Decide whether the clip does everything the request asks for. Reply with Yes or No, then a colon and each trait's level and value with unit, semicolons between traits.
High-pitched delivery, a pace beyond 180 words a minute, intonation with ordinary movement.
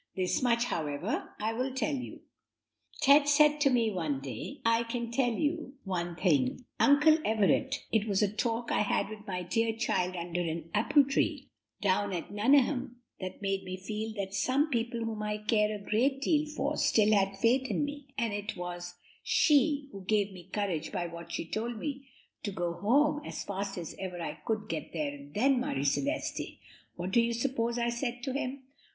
No: high, 220 Hz; average, 195 wpm; wide, 5.9 semitones